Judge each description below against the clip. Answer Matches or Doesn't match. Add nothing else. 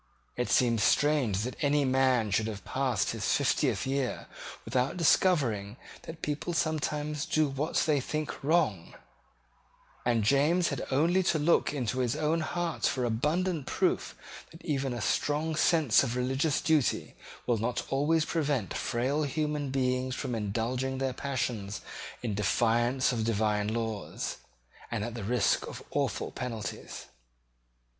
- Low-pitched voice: Matches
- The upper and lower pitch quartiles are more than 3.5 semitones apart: Matches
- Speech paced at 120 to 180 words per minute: Matches